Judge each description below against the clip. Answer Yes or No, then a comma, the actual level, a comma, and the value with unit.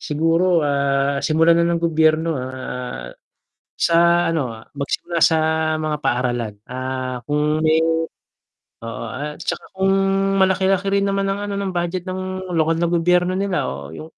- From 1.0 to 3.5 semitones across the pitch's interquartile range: No, average, 4.6 semitones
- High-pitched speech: No, medium, 160 Hz